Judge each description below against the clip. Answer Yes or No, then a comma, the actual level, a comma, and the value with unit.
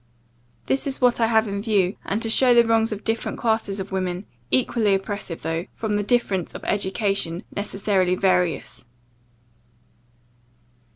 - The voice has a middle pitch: No, high, 205 Hz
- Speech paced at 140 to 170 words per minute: Yes, average, 150 wpm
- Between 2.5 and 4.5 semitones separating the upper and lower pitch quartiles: Yes, average, 3.1 semitones